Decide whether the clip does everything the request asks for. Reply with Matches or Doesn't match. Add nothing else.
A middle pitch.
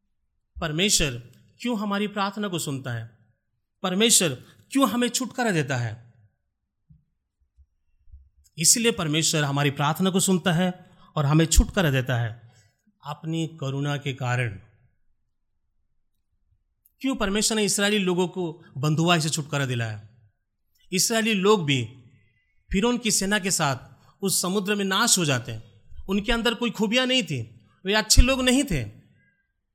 Matches